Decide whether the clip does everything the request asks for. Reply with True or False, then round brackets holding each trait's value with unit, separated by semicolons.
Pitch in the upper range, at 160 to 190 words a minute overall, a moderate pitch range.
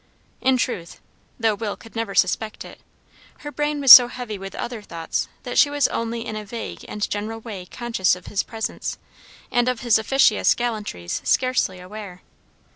True (225 Hz; 175 wpm; 3.2 semitones)